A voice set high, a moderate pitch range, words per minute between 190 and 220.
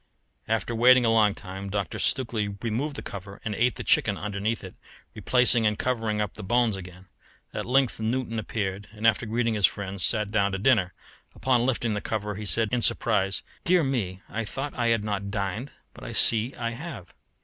No: low, 110 Hz; average, 3.1 semitones; average, 200 wpm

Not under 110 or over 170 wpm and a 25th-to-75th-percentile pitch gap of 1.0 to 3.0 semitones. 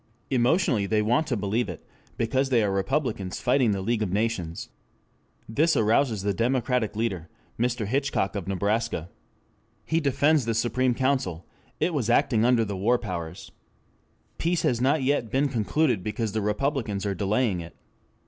No: average, 160 wpm; average, 4.5 semitones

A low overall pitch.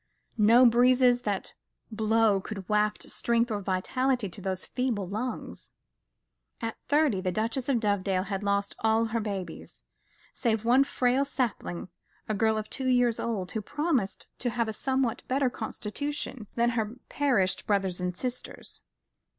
No: high, 225 Hz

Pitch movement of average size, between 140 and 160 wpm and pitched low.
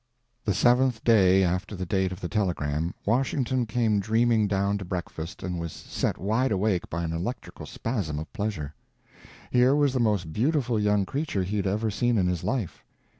No: average, 4.5 semitones; average, 180 wpm; low, 105 Hz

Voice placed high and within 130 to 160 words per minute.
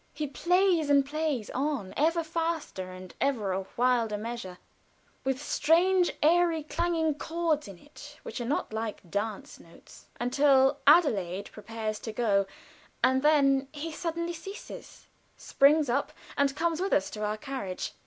Yes: very high, 280 Hz; average, 145 wpm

